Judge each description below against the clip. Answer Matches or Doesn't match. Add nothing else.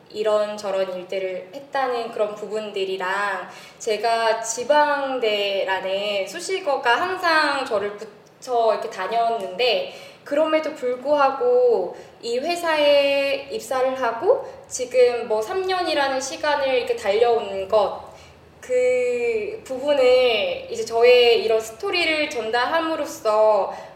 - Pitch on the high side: Matches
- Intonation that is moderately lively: Doesn't match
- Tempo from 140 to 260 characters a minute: Matches